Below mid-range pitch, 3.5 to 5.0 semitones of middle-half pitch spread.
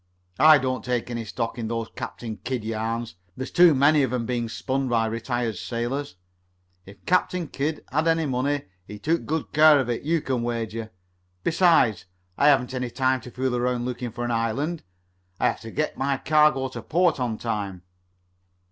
Yes: low, 125 Hz; average, 4.0 semitones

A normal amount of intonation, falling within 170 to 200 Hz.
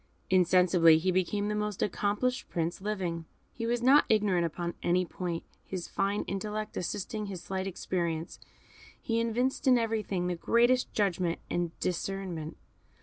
Yes: average, 3.4 semitones; high, 190 Hz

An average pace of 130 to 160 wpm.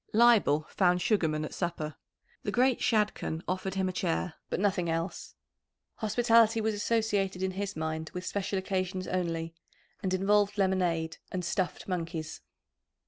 Yes: average, 140 wpm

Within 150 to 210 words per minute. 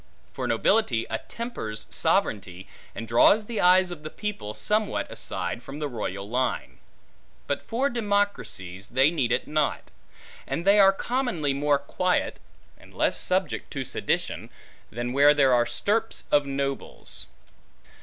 No: average, 140 wpm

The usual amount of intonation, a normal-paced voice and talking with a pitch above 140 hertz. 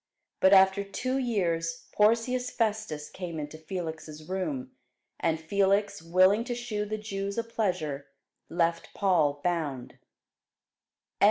No: average, 4.6 semitones; slow, 115 wpm; high, 190 Hz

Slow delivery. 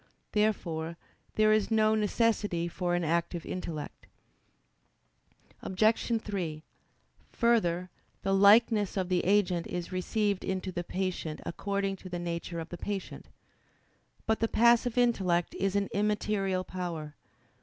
Yes: slow, 125 wpm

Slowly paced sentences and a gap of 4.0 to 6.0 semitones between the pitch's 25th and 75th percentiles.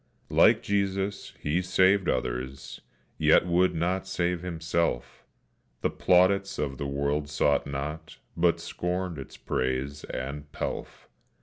Yes: slow, 120 wpm; average, 4.4 semitones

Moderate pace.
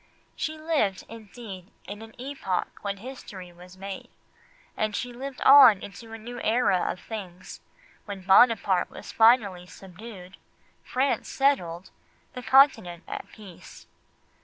No: slow, 130 wpm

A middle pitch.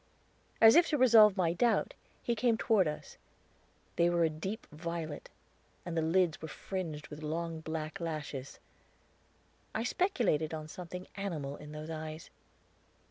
Yes: medium, 165 Hz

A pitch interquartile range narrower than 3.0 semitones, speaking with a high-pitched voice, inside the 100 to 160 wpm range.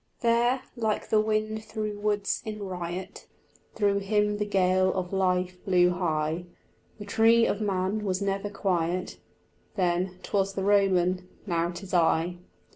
Yes: narrow, 2.5 semitones; high, 195 Hz; average, 140 wpm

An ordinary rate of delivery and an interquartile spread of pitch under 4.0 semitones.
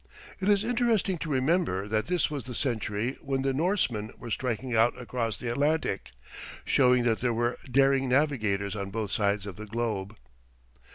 No: average, 170 wpm; average, 4.6 semitones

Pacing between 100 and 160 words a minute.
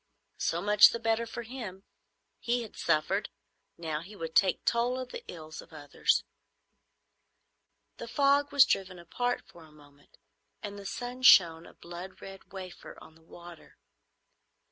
Yes: average, 155 wpm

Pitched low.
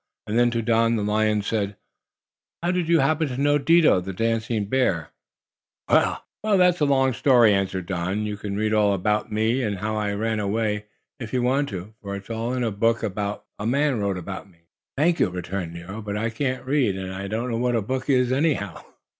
Yes: low, 110 Hz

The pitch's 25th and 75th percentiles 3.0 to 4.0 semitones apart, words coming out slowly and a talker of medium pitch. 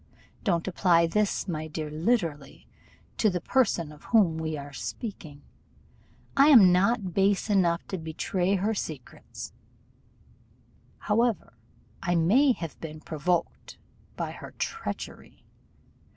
No: average, 4.6 semitones; slow, 120 wpm; medium, 180 Hz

